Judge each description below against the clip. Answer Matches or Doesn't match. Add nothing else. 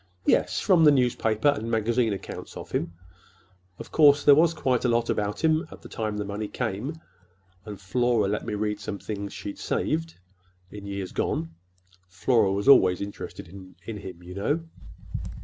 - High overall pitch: Doesn't match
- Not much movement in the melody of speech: Doesn't match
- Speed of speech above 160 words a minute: Matches